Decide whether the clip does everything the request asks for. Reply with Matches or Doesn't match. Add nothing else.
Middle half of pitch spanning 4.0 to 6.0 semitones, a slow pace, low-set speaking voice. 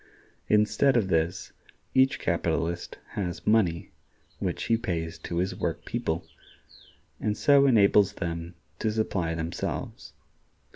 Matches